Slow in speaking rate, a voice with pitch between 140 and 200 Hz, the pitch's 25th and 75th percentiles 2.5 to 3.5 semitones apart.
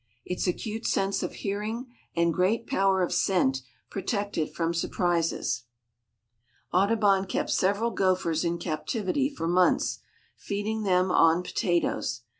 Yes: slow, 125 wpm; medium, 185 Hz; average, 3.2 semitones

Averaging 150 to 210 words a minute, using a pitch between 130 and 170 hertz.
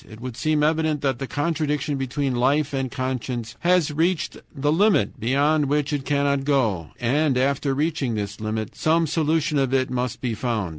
Yes: average, 180 wpm; medium, 140 Hz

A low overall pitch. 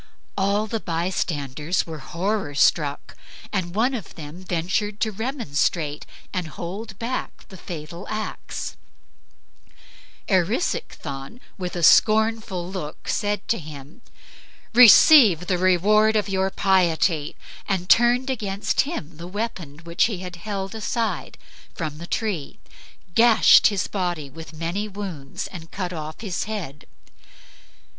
No: medium, 185 Hz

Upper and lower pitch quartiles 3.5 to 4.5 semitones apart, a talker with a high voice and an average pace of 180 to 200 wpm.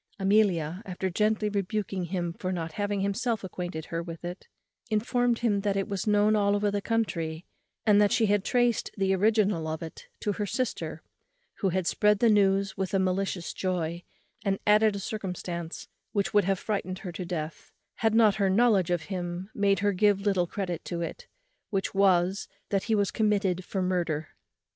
No: average, 2.7 semitones; high, 195 Hz; average, 185 wpm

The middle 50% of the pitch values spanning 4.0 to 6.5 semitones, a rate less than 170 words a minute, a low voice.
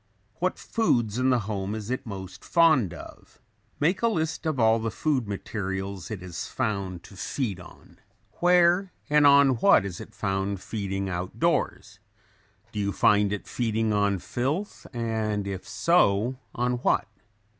Yes: average, 5.0 semitones; average, 155 wpm; low, 110 Hz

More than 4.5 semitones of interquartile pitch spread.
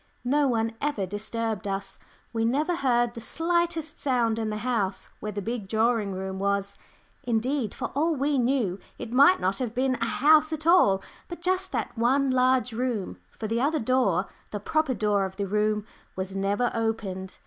Yes: average, 4.9 semitones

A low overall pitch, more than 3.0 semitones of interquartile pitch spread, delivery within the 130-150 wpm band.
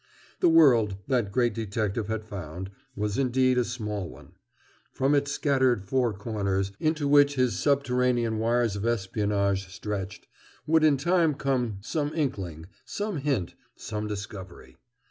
Yes: low, 115 Hz; average, 5.3 semitones; average, 140 wpm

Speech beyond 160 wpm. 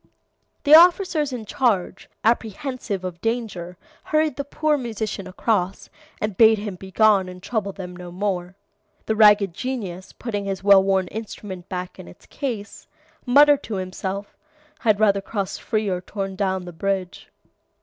No: average, 150 wpm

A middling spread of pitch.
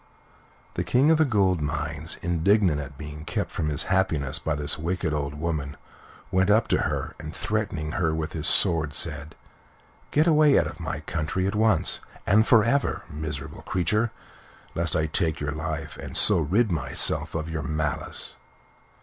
Yes: average, 4.6 semitones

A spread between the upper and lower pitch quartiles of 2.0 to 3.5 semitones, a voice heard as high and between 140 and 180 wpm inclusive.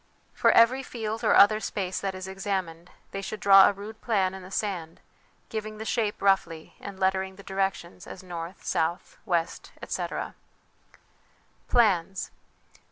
Yes: narrow, 2.4 semitones; high, 195 Hz; average, 150 wpm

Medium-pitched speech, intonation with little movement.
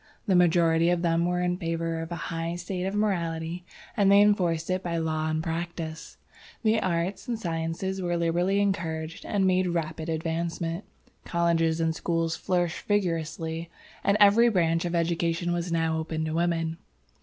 Yes: medium, 170 Hz; narrow, 1.8 semitones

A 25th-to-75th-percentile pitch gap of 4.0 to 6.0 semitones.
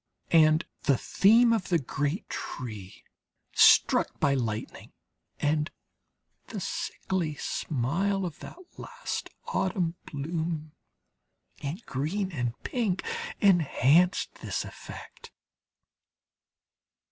Yes: average, 5.2 semitones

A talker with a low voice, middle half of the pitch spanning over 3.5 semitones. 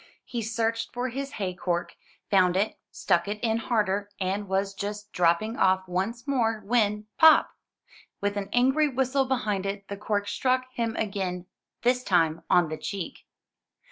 No: high, 210 Hz; average, 3.9 semitones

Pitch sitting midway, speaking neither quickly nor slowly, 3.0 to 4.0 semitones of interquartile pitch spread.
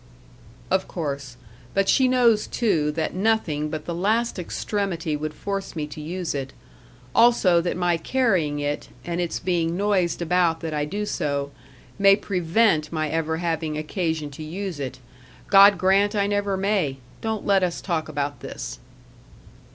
No: medium, 175 Hz; average, 160 wpm; average, 4.4 semitones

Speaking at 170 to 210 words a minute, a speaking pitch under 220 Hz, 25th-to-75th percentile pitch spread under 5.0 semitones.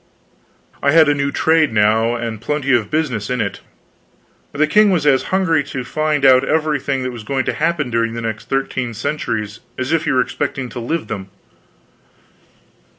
Yes: average, 185 wpm; low, 135 Hz; average, 4.6 semitones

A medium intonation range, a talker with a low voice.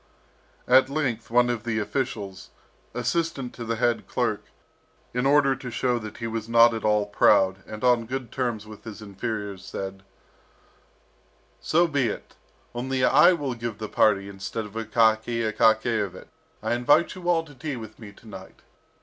Yes: average, 3.2 semitones; low, 115 Hz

